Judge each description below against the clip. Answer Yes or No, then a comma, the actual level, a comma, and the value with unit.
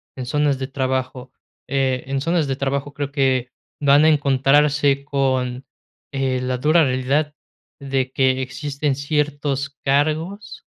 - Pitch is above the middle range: No, medium, 140 Hz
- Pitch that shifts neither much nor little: No, narrow, 1.9 semitones